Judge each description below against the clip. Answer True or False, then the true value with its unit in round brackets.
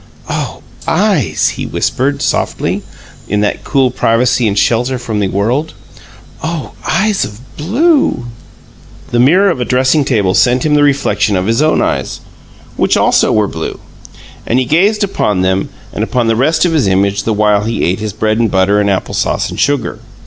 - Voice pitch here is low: True (120 Hz)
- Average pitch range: False (5.9 semitones)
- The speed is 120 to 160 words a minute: False (180 wpm)